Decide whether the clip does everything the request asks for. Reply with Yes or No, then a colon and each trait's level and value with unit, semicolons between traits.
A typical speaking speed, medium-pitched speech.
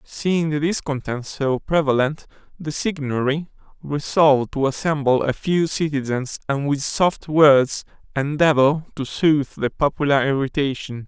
No: slow, 125 wpm; medium, 145 Hz